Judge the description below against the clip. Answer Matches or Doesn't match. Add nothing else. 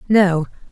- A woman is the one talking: Matches